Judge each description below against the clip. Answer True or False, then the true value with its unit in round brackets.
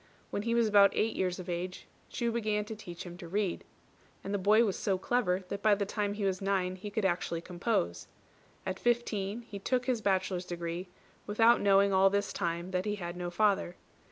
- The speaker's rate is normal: False (210 wpm)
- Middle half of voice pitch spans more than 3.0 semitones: False (2.6 semitones)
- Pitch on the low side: False (195 Hz)